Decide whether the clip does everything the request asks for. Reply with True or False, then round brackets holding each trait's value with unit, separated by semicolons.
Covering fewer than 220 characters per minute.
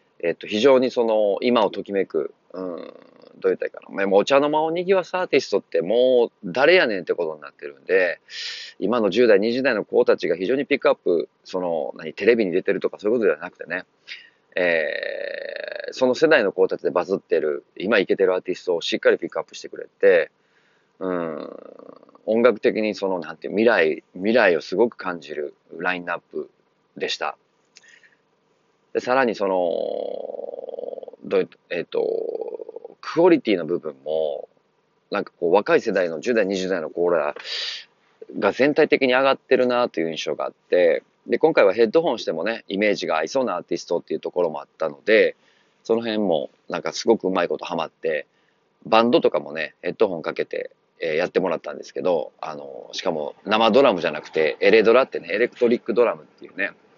False (365 characters per minute)